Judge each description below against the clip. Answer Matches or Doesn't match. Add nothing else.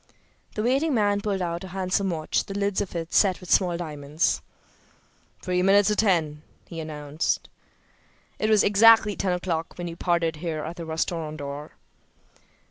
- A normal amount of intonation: Matches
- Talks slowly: Doesn't match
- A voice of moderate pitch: Matches